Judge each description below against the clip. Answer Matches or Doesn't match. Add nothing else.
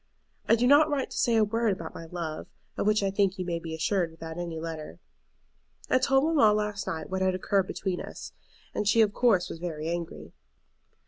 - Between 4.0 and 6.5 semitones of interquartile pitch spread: Matches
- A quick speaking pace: Matches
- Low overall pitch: Doesn't match